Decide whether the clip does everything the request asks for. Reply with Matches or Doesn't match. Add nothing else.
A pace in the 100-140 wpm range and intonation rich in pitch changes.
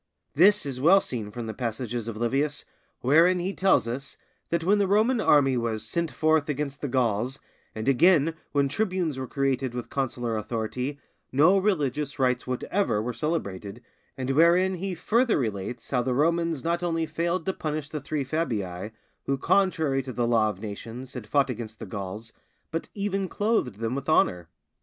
Doesn't match